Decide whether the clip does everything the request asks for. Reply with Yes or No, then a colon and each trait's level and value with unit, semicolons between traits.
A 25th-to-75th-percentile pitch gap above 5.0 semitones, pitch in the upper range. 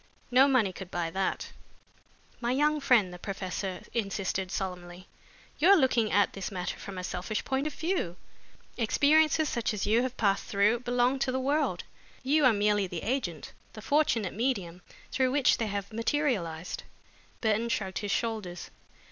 Yes: wide, 5.5 semitones; high, 220 Hz